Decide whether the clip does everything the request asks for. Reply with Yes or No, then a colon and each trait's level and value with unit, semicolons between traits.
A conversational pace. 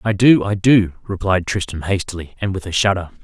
Yes: average, 185 wpm